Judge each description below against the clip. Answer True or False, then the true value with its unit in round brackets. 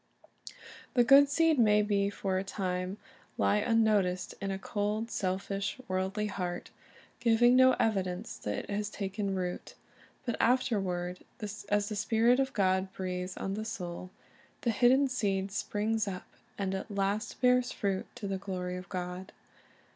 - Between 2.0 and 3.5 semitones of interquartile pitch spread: True (3.0 semitones)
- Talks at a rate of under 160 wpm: True (145 wpm)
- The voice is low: False (200 Hz)